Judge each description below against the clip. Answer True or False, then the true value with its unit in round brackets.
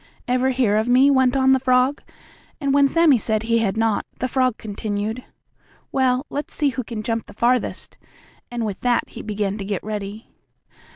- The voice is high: True (245 Hz)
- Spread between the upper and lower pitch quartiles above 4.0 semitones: False (3.4 semitones)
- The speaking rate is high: False (185 wpm)